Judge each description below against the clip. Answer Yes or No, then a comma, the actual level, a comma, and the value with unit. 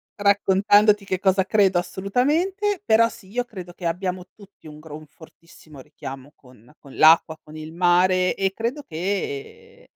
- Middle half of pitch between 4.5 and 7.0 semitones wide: Yes, average, 5.1 semitones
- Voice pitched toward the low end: No, high, 190 Hz